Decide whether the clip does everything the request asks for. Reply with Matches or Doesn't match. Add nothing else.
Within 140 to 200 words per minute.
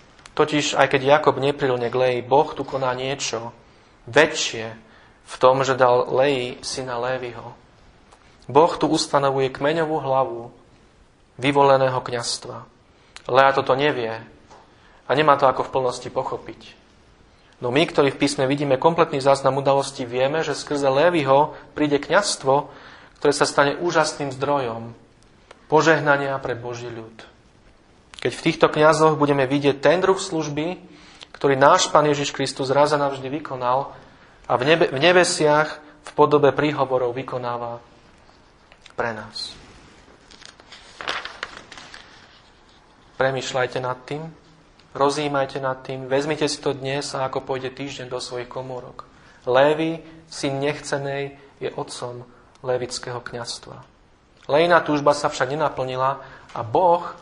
Doesn't match